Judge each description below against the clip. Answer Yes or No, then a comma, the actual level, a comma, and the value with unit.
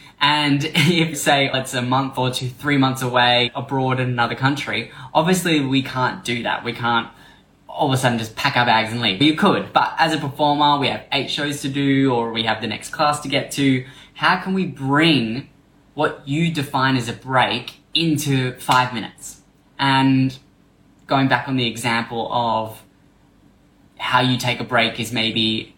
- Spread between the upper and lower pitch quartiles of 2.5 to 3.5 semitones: Yes, average, 3.2 semitones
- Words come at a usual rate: Yes, average, 185 wpm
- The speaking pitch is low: Yes, low, 130 Hz